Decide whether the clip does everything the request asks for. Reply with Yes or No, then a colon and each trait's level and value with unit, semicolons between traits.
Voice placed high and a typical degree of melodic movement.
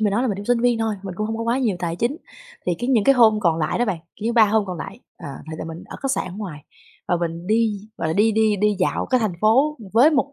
Yes: high, 215 Hz; average, 4.5 semitones